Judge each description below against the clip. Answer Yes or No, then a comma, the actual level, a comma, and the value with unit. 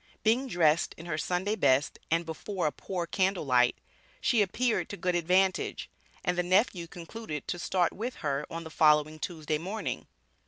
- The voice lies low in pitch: No, medium, 175 Hz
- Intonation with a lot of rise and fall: No, average, 3.7 semitones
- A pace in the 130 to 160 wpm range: No, average, 170 wpm